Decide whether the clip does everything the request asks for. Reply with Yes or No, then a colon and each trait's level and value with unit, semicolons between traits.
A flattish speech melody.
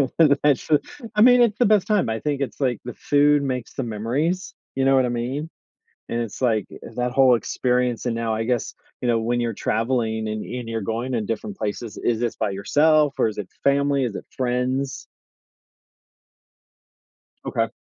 No: average, 3.7 semitones